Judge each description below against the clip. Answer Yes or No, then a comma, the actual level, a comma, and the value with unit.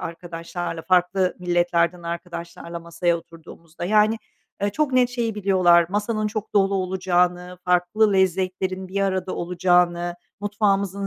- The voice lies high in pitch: No, medium, 180 Hz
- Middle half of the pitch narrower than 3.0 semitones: Yes, narrow, 2.4 semitones